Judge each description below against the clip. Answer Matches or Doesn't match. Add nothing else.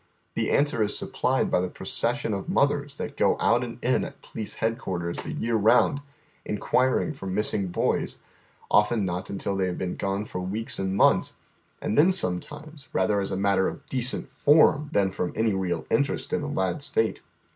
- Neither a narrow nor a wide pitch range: Doesn't match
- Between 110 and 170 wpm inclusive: Doesn't match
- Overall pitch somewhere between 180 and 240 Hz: Doesn't match